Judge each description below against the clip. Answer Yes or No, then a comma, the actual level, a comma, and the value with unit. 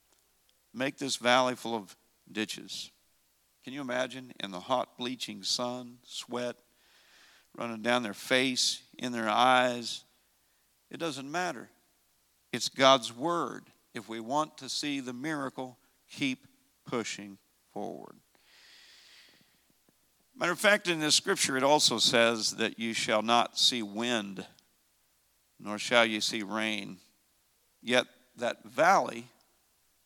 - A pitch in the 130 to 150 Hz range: No, low, 120 Hz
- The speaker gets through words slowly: Yes, slow, 120 wpm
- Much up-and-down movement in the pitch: No, average, 2.7 semitones